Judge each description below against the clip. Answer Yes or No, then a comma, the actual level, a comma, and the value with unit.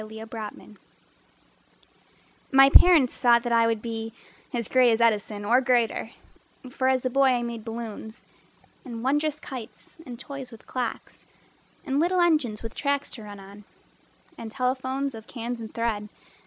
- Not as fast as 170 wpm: Yes, average, 155 wpm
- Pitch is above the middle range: Yes, high, 240 Hz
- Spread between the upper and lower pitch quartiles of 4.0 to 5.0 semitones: No, average, 3.1 semitones